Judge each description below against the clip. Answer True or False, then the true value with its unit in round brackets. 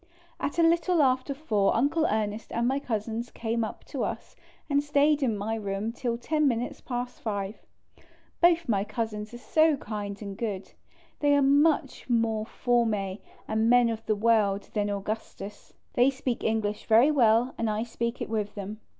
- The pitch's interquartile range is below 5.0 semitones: True (4.1 semitones)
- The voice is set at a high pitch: True (230 Hz)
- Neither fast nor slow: True (175 wpm)